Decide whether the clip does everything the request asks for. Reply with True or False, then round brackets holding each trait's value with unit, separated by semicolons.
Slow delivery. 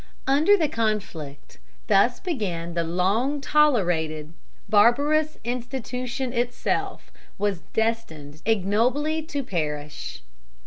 True (90 wpm)